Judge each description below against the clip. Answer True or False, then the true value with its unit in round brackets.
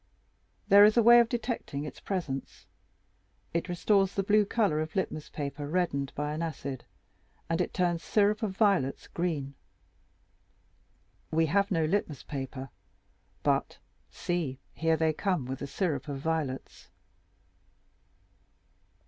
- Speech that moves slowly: True (130 wpm)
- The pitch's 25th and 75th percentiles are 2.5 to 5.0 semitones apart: False (5.5 semitones)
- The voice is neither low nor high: True (165 Hz)